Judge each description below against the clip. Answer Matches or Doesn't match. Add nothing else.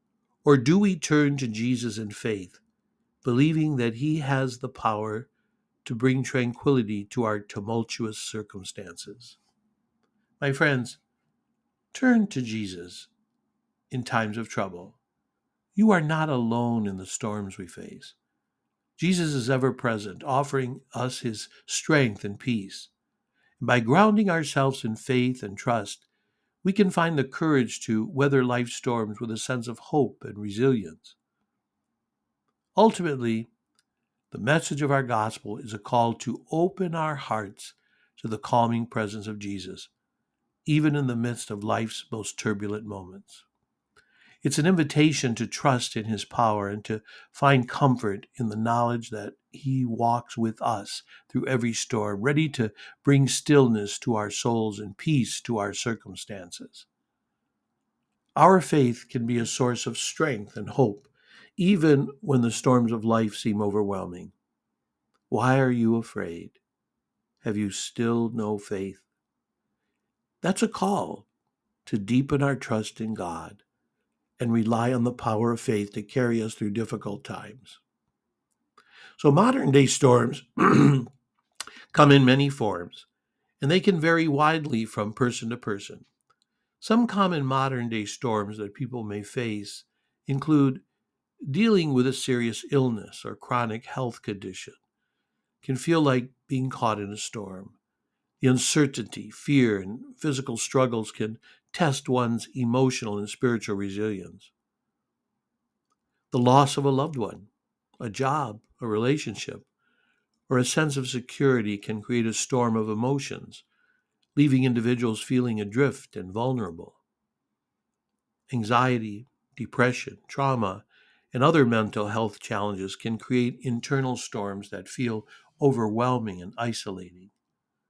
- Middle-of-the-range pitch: Doesn't match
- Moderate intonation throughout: Matches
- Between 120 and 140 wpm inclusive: Matches